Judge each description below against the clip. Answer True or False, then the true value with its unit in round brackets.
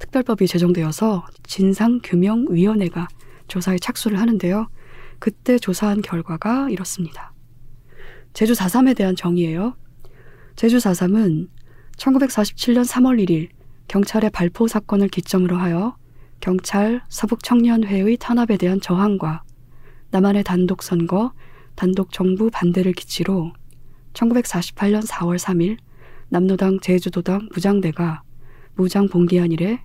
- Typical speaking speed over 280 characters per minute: False (245 characters per minute)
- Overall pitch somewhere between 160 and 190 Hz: True (185 Hz)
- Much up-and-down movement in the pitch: False (4.1 semitones)